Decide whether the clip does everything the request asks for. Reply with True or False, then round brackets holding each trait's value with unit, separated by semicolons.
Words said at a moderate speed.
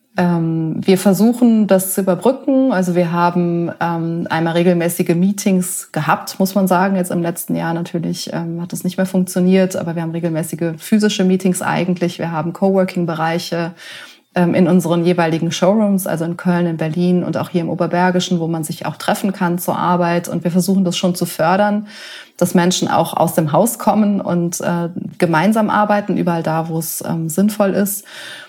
True (170 wpm)